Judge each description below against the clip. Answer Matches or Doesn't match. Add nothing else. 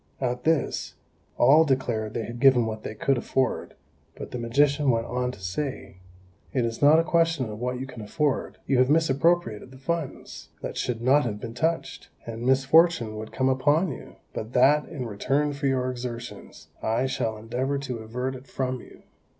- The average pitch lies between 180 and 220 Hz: Doesn't match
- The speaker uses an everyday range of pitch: Matches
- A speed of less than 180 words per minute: Doesn't match